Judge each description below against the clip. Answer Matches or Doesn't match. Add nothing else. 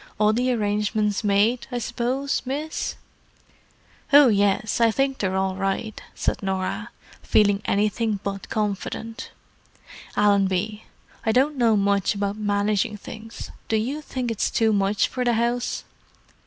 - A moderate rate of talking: Doesn't match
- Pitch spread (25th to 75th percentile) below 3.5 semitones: Matches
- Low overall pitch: Doesn't match